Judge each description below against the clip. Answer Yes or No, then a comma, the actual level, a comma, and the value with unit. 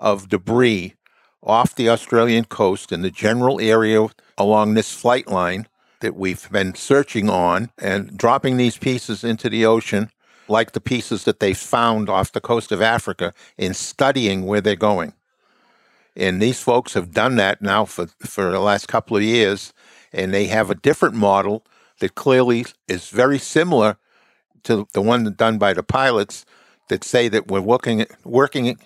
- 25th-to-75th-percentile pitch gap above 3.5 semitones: No, average, 3.0 semitones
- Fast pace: No, average, 165 wpm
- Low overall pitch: Yes, low, 110 Hz